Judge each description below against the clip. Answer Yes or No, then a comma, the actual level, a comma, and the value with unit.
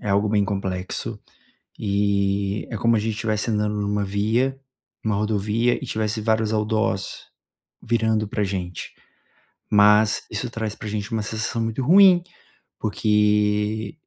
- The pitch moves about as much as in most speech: No, narrow, 1.4 semitones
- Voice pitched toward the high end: No, low, 105 Hz